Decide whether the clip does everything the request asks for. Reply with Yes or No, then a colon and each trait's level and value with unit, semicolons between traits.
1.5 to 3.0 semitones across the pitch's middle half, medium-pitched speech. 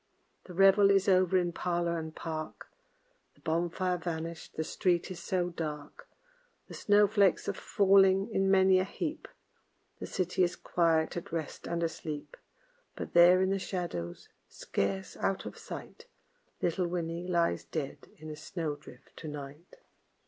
Yes: average, 2.7 semitones; medium, 175 Hz